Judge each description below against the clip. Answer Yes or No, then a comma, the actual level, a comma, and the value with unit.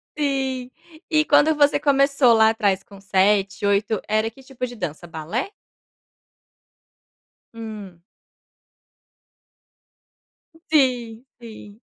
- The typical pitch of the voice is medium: No, high, 225 Hz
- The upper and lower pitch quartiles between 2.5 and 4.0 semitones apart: No, average, 4.9 semitones